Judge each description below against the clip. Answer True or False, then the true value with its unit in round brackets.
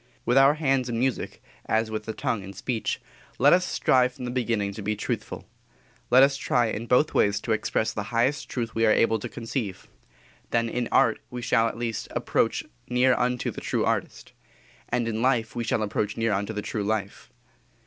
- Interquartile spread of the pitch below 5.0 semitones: True (2.4 semitones)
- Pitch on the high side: False (115 Hz)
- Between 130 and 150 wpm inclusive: False (200 wpm)